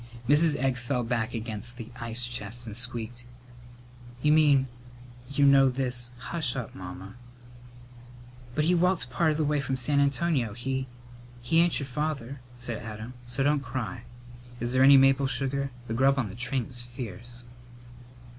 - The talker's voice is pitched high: No, low, 125 Hz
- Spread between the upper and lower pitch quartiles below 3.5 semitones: Yes, average, 2.7 semitones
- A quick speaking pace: No, average, 165 wpm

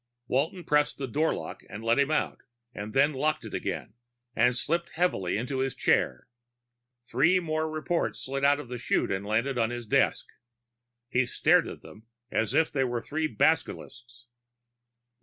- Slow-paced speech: No, average, 160 wpm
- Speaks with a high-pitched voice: No, low, 135 Hz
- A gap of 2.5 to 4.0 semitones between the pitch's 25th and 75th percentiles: No, average, 4.6 semitones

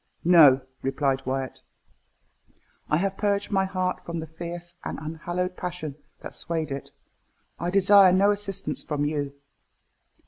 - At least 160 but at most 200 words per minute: No, slow, 135 wpm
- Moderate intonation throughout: Yes, average, 4.1 semitones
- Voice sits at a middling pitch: Yes, medium, 170 Hz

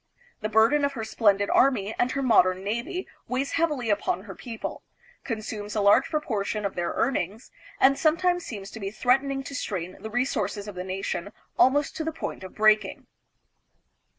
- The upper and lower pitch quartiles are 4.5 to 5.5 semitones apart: Yes, average, 5.2 semitones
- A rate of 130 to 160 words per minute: No, average, 175 wpm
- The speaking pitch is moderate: No, high, 220 Hz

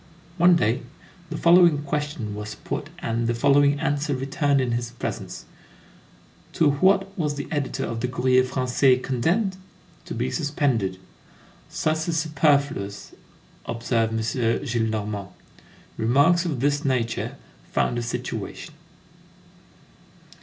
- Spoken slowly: Yes, slow, 120 wpm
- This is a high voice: No, low, 135 Hz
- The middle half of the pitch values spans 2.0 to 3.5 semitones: No, average, 4.3 semitones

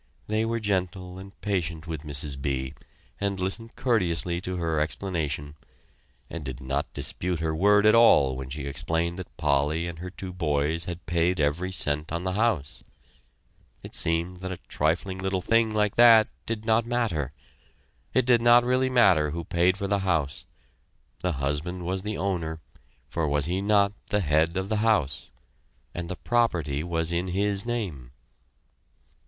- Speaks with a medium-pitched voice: No, very low, 90 Hz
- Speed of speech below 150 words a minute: No, average, 170 wpm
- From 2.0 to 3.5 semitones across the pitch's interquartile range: No, average, 4.7 semitones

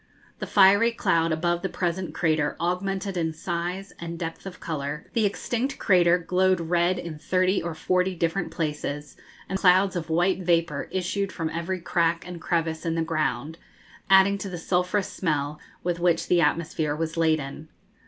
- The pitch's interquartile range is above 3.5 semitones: No, narrow, 2.4 semitones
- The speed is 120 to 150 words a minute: No, average, 165 wpm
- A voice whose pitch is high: No, medium, 170 Hz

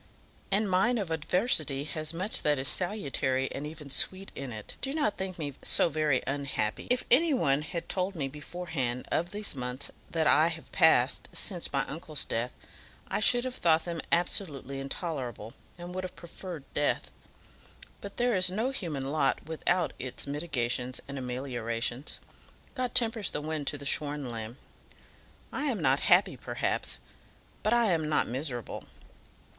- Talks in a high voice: No, medium, 155 Hz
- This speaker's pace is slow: No, average, 160 wpm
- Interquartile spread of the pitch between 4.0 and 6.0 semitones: Yes, average, 5.2 semitones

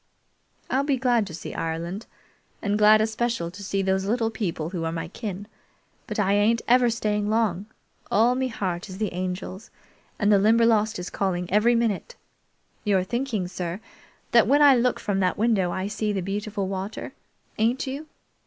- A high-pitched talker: Yes, high, 210 Hz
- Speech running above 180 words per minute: No, average, 175 wpm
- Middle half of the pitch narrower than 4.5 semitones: Yes, average, 3.6 semitones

